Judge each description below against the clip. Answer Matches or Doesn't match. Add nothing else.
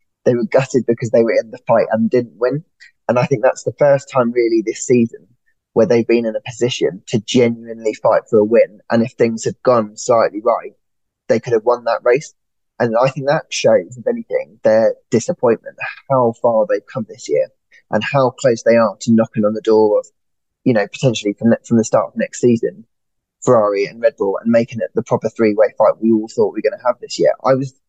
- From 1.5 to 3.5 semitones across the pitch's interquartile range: Matches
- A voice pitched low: Matches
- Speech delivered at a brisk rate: Matches